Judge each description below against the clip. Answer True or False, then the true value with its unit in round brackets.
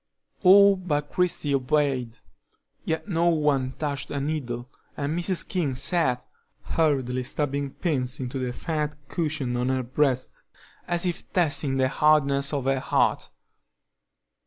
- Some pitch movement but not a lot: True (3.6 semitones)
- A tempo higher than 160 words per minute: False (135 wpm)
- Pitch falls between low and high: True (145 Hz)